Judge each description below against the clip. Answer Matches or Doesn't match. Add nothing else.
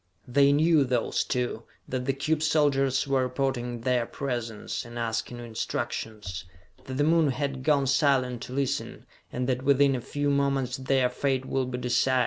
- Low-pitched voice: Matches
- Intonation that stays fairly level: Matches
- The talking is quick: Doesn't match